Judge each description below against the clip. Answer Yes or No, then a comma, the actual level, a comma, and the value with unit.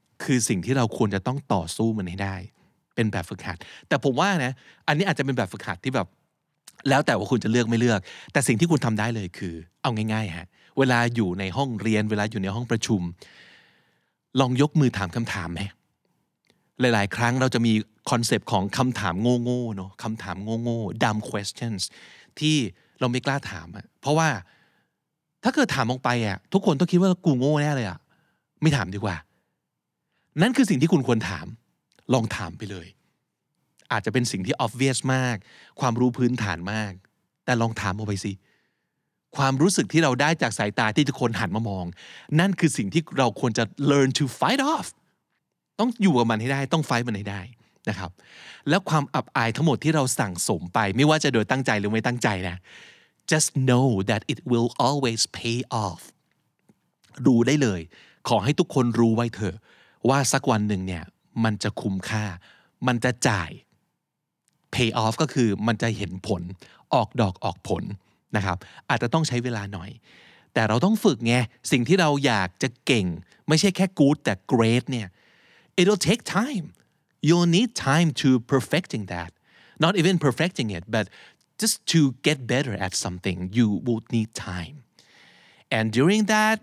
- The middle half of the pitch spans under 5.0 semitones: No, average, 5.3 semitones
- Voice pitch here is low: Yes, low, 120 Hz